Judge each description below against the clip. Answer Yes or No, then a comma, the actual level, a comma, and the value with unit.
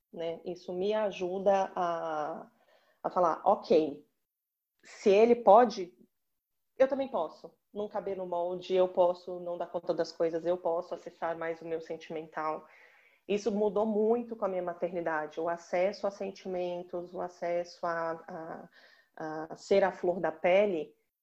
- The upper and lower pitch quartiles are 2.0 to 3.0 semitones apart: Yes, average, 2.7 semitones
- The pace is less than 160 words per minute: Yes, average, 150 wpm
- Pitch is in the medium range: Yes, medium, 180 Hz